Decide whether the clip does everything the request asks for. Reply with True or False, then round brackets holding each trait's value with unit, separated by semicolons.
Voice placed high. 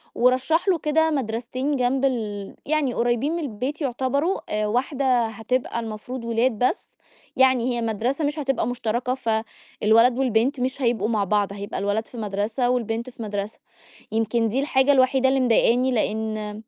True (245 Hz)